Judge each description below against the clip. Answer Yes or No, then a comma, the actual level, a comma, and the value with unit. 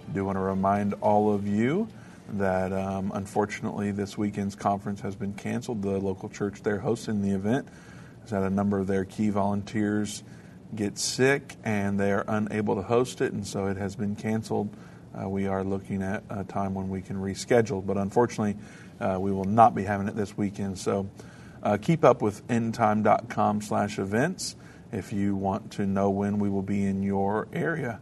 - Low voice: Yes, low, 100 Hz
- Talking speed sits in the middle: Yes, average, 190 wpm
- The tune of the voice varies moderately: No, narrow, 1.4 semitones